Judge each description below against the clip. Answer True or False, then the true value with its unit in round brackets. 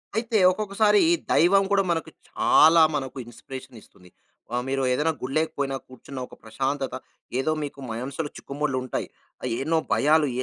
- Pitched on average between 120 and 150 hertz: True (140 Hz)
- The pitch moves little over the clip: False (3.8 semitones)